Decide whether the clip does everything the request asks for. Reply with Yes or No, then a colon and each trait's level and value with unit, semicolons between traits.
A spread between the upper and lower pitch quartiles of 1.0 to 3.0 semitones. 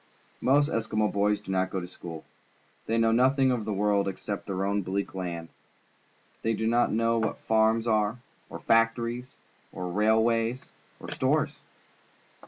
Yes: average, 2.7 semitones